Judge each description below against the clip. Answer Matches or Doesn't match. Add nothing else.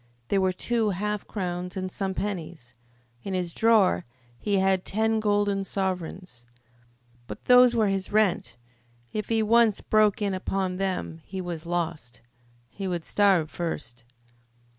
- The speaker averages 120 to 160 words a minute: Matches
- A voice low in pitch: Doesn't match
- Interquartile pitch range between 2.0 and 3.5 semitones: Matches